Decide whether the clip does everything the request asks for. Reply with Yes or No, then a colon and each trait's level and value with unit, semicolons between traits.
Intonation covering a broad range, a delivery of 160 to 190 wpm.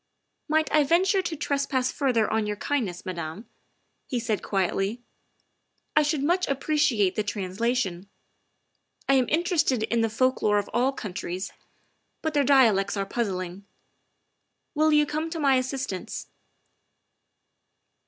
No: wide, 6.4 semitones; average, 145 wpm